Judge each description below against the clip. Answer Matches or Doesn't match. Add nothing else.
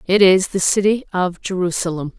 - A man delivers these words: Doesn't match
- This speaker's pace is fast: Doesn't match